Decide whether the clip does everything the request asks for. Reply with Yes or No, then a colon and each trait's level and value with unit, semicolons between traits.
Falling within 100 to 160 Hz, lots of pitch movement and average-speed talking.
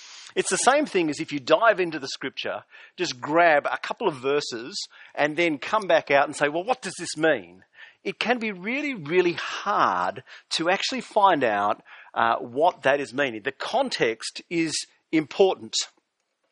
No: medium, 175 Hz; wide, 7.9 semitones; average, 175 wpm